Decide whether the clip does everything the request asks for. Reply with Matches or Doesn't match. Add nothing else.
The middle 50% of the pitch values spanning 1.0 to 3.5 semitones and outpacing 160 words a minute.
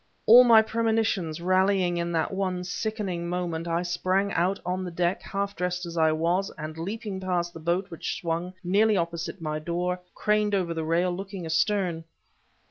Matches